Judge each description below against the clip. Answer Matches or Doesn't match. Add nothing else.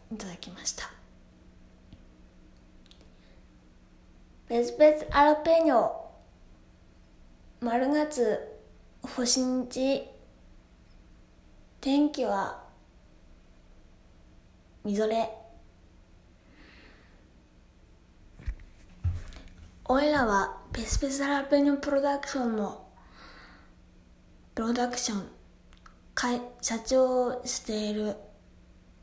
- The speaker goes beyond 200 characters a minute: Doesn't match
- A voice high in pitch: Matches